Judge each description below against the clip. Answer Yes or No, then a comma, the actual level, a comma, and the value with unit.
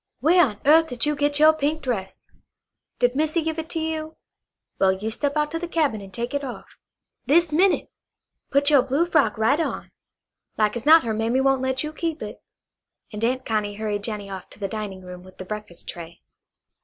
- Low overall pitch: No, very high, 260 Hz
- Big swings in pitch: Yes, wide, 6.6 semitones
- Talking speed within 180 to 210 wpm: Yes, fast, 205 wpm